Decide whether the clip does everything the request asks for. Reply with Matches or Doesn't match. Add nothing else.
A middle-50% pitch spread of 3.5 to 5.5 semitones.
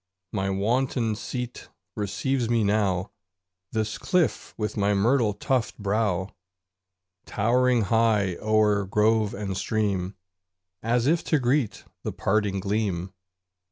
Doesn't match